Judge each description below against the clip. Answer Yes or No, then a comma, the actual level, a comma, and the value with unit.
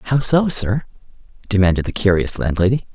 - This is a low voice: Yes, low, 105 Hz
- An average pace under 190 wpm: Yes, average, 140 wpm